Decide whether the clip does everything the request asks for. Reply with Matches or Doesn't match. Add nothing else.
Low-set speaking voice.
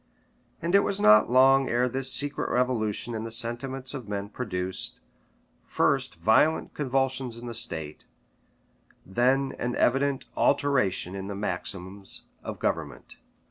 Matches